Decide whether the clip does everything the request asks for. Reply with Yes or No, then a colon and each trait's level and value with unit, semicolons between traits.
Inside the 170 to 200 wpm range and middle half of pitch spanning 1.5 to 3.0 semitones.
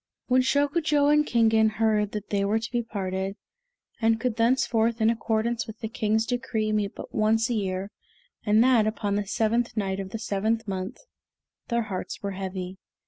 Yes: average, 180 wpm; narrow, 2.6 semitones